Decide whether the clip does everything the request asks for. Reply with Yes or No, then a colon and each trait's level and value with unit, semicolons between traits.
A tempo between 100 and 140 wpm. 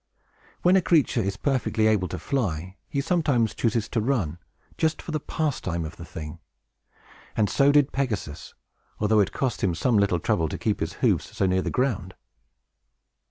No: average, 175 wpm